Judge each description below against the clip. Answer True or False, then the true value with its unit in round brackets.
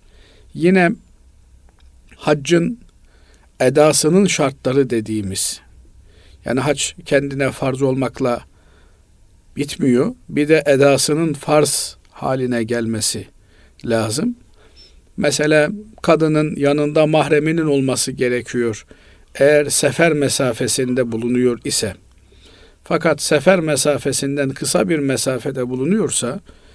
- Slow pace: True (80 wpm)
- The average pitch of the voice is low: True (130 Hz)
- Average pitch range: False (6.2 semitones)